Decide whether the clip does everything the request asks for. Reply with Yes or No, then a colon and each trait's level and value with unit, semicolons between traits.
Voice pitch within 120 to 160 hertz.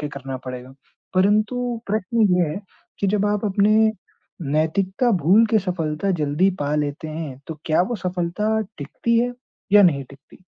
No: medium, 185 Hz